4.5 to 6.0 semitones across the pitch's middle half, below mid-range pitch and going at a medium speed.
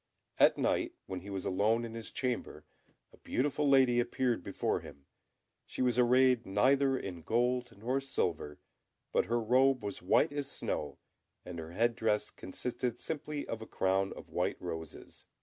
Yes: average, 4.9 semitones; low, 115 Hz; average, 165 wpm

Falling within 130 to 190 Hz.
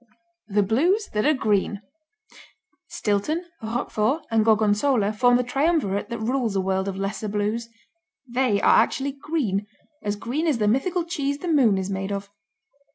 No: high, 225 Hz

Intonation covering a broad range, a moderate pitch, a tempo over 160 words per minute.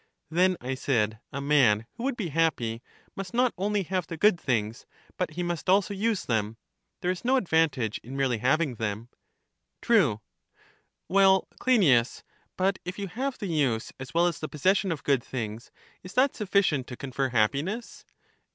Yes: wide, 7.6 semitones; medium, 160 Hz; average, 170 wpm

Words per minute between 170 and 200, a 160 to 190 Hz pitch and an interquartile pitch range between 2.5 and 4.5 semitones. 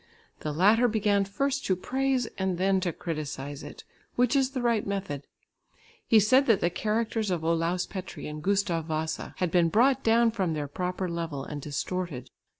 No: average, 175 wpm; medium, 185 Hz; wide, 5.4 semitones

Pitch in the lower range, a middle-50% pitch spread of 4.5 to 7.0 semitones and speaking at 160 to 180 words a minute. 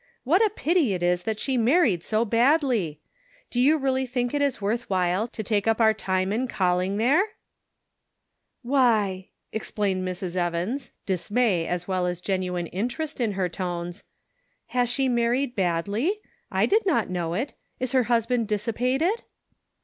No: high, 220 Hz; wide, 5.6 semitones; average, 170 wpm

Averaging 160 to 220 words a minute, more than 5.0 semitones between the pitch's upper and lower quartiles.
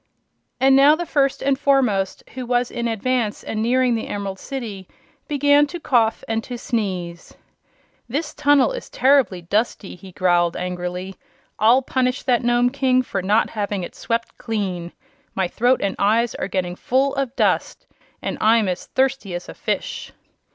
Yes: average, 165 wpm; wide, 5.4 semitones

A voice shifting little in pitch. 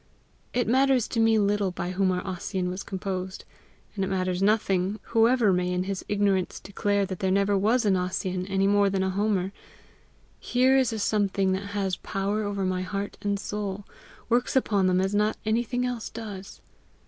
Yes: narrow, 2.2 semitones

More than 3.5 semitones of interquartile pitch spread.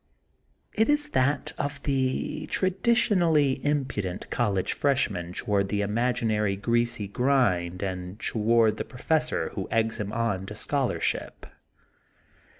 Yes: wide, 5.6 semitones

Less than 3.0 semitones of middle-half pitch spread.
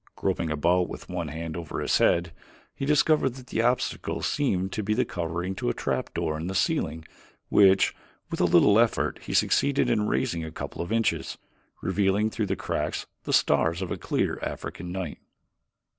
No: average, 5.1 semitones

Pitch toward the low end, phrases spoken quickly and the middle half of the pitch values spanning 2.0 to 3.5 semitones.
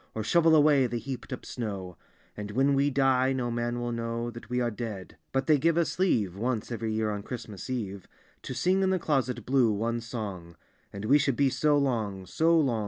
No: low, 120 Hz; fast, 215 wpm; average, 4.0 semitones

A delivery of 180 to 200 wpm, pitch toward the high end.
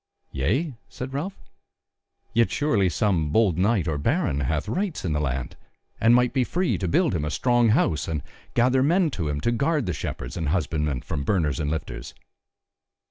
No: average, 185 wpm; very low, 95 Hz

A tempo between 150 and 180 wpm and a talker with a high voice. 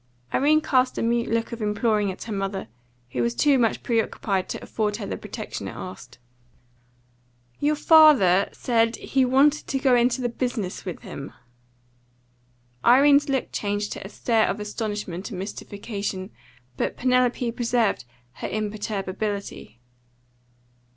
No: average, 140 wpm; high, 220 Hz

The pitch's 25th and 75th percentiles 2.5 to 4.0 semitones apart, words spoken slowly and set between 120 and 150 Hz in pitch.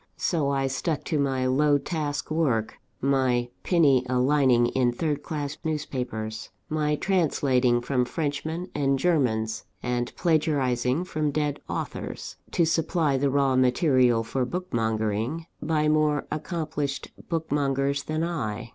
Yes: average, 3.6 semitones; slow, 130 wpm; medium, 140 Hz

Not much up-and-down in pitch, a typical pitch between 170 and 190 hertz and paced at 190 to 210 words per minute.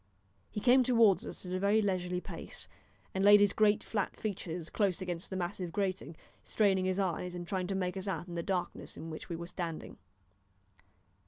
Yes: narrow, 2.3 semitones; medium, 185 Hz; average, 195 wpm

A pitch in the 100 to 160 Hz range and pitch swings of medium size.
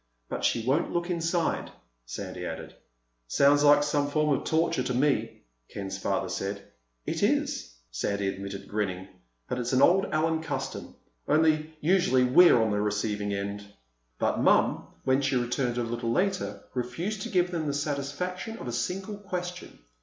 No: medium, 140 Hz; wide, 6.9 semitones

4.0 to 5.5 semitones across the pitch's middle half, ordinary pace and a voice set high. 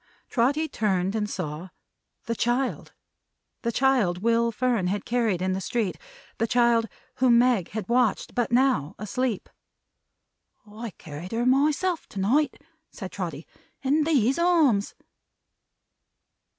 No: average, 4.7 semitones; slow, 125 wpm; high, 230 Hz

